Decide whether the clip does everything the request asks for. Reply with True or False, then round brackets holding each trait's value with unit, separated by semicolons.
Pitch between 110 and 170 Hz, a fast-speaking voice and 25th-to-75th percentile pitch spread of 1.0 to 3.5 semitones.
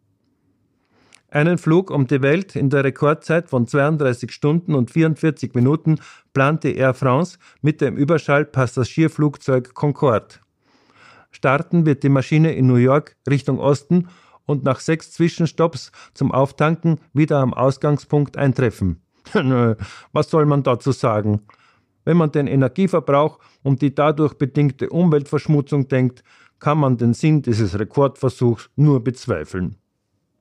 False (140 Hz; 130 wpm; 2.9 semitones)